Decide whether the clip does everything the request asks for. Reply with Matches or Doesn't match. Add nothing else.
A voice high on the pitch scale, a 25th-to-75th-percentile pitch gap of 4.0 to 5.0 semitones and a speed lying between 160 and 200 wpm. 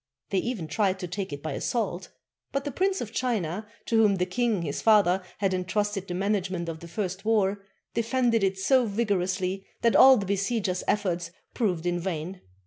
Doesn't match